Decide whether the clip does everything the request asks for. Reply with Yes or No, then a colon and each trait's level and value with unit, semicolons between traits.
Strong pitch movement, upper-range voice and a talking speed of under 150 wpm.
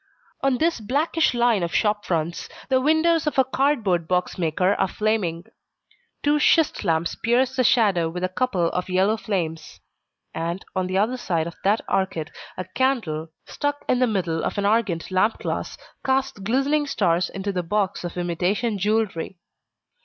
No: wide, 6.2 semitones; high, 200 Hz; average, 170 wpm